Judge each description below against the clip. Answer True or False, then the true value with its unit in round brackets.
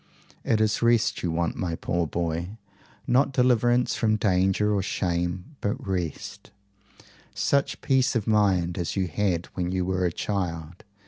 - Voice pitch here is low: True (95 Hz)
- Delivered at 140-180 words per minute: True (150 wpm)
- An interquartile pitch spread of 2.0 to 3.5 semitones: False (4.1 semitones)